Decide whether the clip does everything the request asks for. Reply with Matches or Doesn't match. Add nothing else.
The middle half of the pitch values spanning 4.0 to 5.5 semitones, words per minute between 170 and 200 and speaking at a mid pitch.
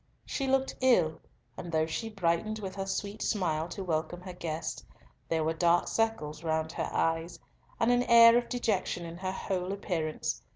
Matches